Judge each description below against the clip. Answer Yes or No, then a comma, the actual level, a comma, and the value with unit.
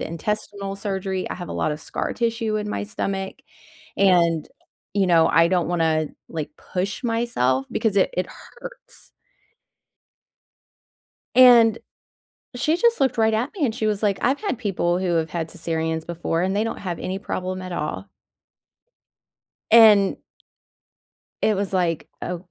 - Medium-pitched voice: No, high, 195 Hz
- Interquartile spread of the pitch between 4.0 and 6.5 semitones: Yes, average, 4.4 semitones